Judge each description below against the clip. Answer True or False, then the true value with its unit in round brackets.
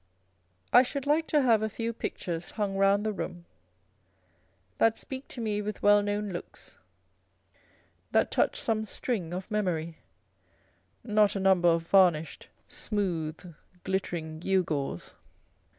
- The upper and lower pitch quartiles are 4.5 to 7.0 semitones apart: False (3.9 semitones)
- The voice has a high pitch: True (200 Hz)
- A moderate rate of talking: False (130 wpm)